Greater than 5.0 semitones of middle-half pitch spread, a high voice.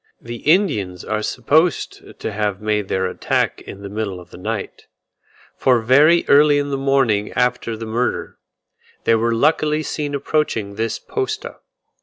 No: wide, 5.5 semitones; low, 120 Hz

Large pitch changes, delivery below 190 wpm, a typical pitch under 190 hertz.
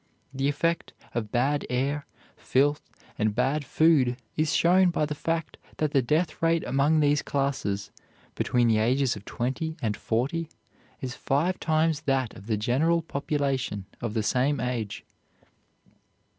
No: average, 4.2 semitones; average, 145 wpm; medium, 140 Hz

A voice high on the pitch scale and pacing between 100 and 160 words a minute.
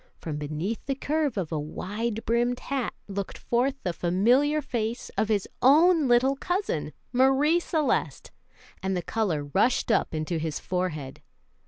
Yes: high, 230 Hz; average, 150 wpm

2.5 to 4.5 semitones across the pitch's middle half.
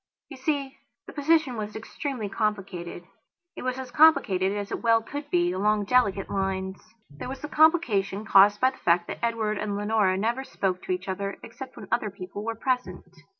No: average, 4.9 semitones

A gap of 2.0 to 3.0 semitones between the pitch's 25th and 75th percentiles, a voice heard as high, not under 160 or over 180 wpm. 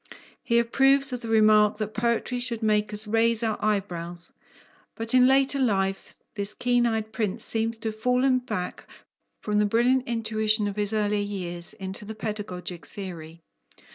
Yes: narrow, 2.4 semitones; high, 215 Hz; average, 165 wpm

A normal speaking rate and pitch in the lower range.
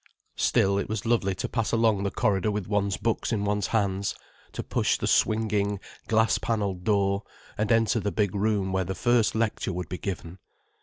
Yes: average, 190 wpm; low, 105 Hz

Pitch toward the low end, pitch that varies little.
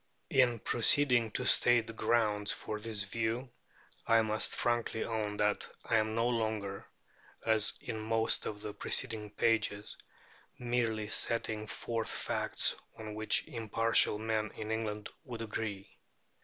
Yes: low, 110 Hz; narrow, 1.3 semitones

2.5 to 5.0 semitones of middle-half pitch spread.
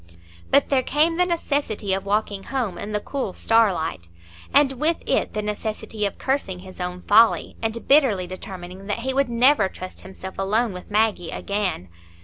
No: wide, 5.5 semitones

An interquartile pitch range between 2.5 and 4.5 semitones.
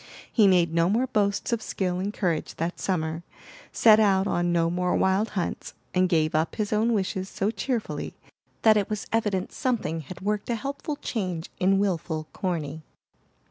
Yes: average, 3.7 semitones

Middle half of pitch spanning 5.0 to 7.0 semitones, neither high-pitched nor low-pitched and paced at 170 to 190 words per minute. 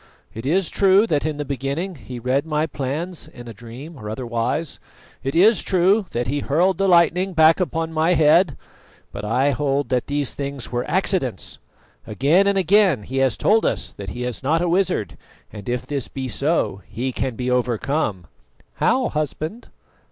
Yes: wide, 5.6 semitones; medium, 145 Hz; average, 180 wpm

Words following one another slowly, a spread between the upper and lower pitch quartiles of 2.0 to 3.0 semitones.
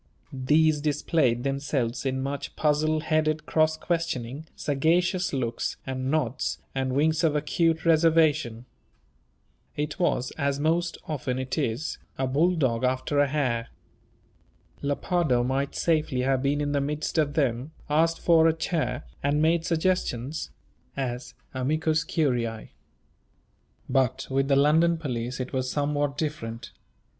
No: slow, 130 wpm; average, 3.4 semitones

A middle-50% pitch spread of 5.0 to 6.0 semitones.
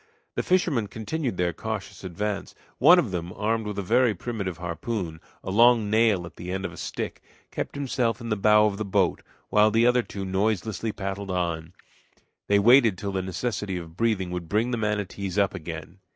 No: average, 3.4 semitones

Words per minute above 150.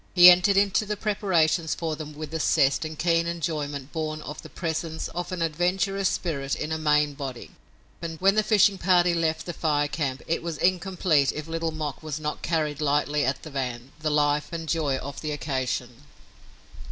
Yes: average, 190 wpm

